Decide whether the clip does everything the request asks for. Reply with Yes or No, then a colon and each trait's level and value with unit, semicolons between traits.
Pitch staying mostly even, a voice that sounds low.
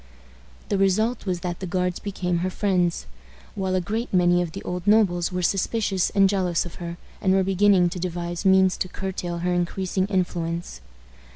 No: narrow, 1.6 semitones; medium, 185 Hz